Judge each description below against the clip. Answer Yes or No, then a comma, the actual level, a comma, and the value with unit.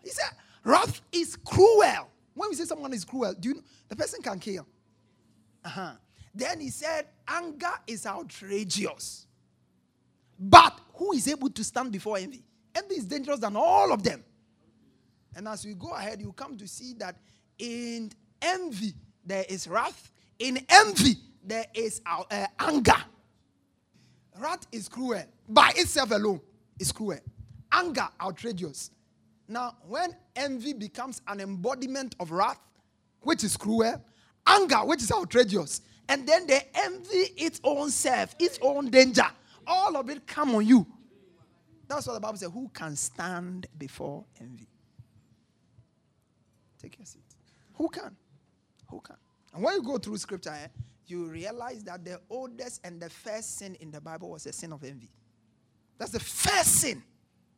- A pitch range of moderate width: No, wide, 7.6 semitones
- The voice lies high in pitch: Yes, high, 225 Hz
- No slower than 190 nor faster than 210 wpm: No, average, 155 wpm